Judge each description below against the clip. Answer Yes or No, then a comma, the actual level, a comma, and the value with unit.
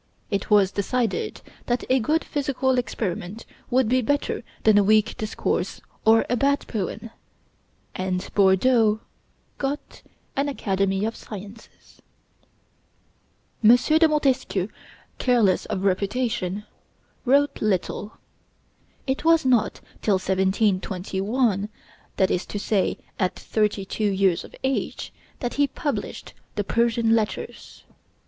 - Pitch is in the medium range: No, high, 220 Hz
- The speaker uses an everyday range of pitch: Yes, average, 4.5 semitones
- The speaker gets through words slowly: Yes, slow, 115 wpm